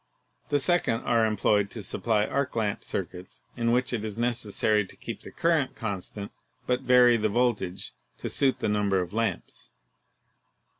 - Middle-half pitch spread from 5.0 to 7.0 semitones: No, average, 3.2 semitones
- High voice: No, low, 110 Hz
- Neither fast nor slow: Yes, average, 160 wpm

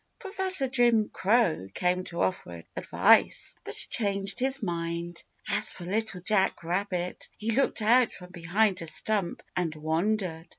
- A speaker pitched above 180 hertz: Yes, high, 190 Hz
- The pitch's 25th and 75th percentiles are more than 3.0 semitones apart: Yes, average, 4.3 semitones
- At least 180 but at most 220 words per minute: No, average, 140 wpm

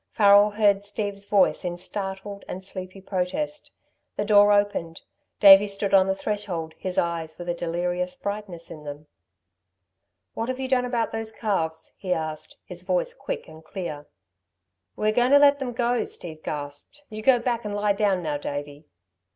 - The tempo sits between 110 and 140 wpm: No, average, 175 wpm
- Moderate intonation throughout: Yes, average, 3.8 semitones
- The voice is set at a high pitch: Yes, high, 200 Hz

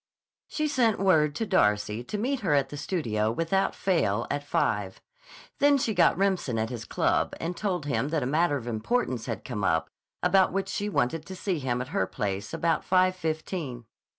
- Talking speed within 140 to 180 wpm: No, average, 195 wpm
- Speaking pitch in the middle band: Yes, medium, 155 Hz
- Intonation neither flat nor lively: No, wide, 8.1 semitones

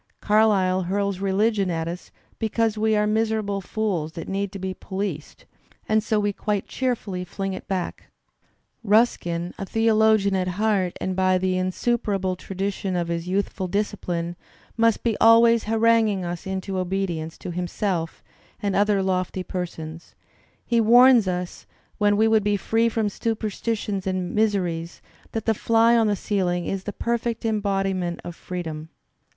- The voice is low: No, high, 195 Hz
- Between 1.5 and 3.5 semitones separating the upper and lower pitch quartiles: Yes, average, 3.1 semitones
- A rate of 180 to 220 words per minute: No, average, 150 wpm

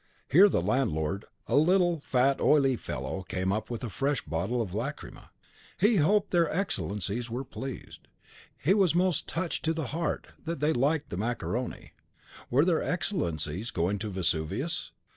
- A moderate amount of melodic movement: No, wide, 8.7 semitones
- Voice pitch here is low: Yes, low, 130 Hz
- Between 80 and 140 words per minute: No, average, 160 wpm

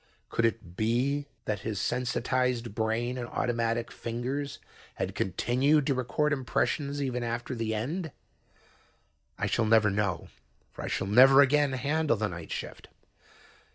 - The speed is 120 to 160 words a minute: Yes, average, 140 wpm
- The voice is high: No, low, 120 Hz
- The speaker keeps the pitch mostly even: No, average, 3.7 semitones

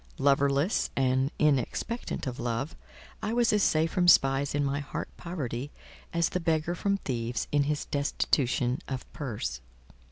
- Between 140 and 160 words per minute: Yes, average, 150 wpm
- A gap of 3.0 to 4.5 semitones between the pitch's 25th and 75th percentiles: Yes, average, 4.0 semitones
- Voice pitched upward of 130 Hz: Yes, medium, 140 Hz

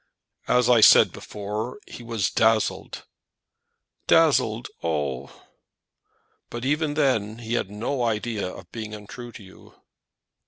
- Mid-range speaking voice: No, low, 115 Hz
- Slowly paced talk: Yes, slow, 125 wpm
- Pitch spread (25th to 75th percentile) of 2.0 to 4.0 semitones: Yes, average, 2.9 semitones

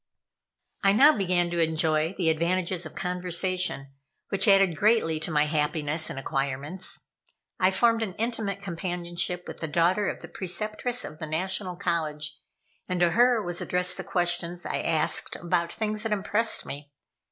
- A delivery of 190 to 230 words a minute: No, average, 160 wpm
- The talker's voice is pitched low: No, medium, 175 Hz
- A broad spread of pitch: No, average, 3.4 semitones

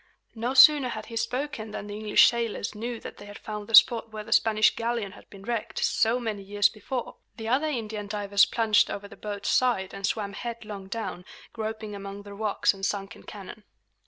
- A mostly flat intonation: Yes, narrow, 2.2 semitones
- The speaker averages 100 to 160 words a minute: No, average, 200 wpm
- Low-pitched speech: No, high, 215 Hz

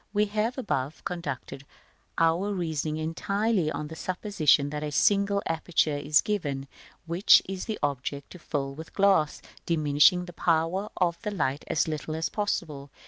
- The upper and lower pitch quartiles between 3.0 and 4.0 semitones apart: No, average, 4.9 semitones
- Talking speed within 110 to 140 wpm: No, average, 160 wpm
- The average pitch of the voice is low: No, medium, 165 Hz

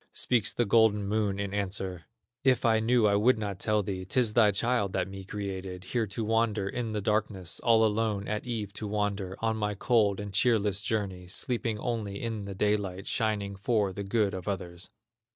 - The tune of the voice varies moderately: No, narrow, 2.3 semitones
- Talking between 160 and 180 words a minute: No, average, 190 wpm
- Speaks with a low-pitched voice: Yes, low, 105 Hz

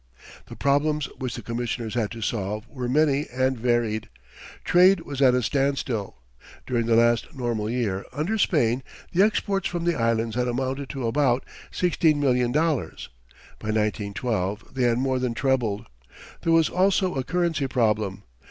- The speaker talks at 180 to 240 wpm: No, average, 160 wpm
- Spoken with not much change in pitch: No, average, 4.2 semitones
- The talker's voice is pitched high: No, low, 125 Hz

